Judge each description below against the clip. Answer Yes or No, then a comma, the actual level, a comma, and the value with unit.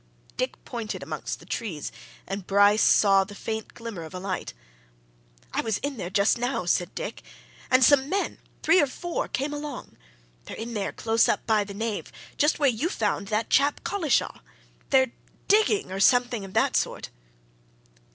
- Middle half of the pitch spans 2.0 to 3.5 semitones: No, wide, 5.4 semitones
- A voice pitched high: Yes, high, 225 Hz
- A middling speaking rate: Yes, average, 170 wpm